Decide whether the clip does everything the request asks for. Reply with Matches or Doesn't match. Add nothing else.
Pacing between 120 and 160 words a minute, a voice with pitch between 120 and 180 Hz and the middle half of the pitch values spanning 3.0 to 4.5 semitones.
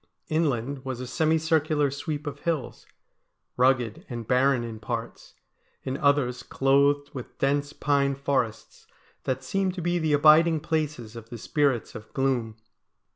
Matches